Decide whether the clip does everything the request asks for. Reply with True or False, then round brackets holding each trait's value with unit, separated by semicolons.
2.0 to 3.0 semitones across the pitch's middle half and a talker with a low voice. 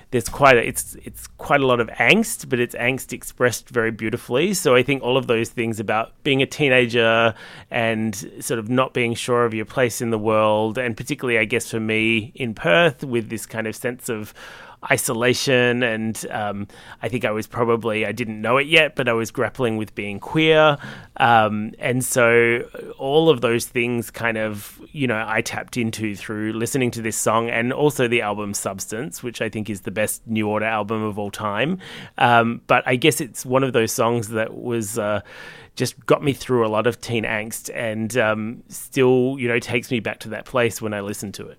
True (2.4 semitones; 115 Hz)